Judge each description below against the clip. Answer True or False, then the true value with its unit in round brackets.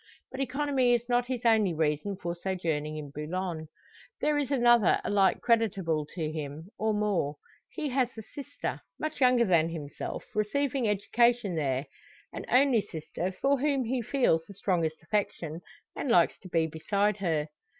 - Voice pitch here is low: False (200 Hz)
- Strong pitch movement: True (7.0 semitones)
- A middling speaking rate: True (160 wpm)